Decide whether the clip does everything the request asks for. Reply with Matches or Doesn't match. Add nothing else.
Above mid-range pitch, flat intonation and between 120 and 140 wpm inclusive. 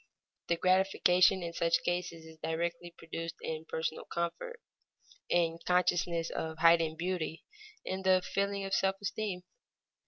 Doesn't match